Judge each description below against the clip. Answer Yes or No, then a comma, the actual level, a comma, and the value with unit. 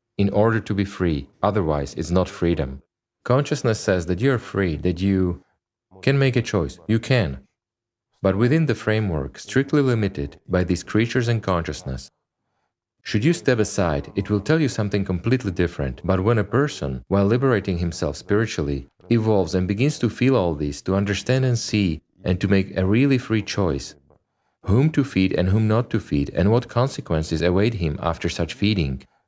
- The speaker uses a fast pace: No, average, 180 wpm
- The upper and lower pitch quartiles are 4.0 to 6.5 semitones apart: Yes, average, 5.3 semitones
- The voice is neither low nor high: No, low, 100 Hz